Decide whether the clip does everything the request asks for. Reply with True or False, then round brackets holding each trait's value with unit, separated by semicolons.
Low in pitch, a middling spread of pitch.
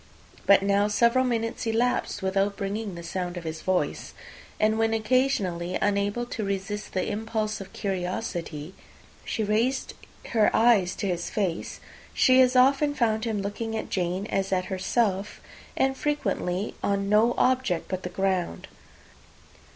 False (205 Hz; 3.4 semitones)